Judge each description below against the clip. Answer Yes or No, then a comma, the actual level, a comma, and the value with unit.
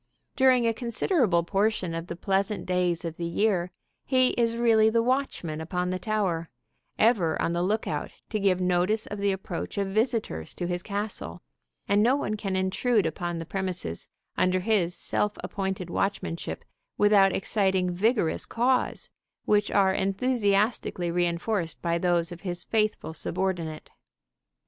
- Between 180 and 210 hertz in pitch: Yes, high, 190 Hz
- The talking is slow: No, average, 150 wpm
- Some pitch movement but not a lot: Yes, average, 3.7 semitones